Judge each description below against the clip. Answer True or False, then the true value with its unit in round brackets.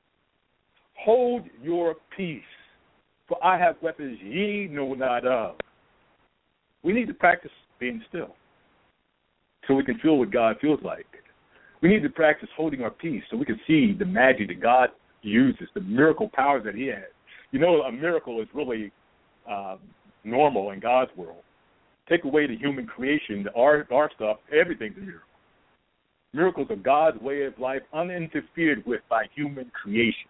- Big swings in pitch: True (6.0 semitones)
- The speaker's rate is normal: True (160 wpm)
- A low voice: False (145 Hz)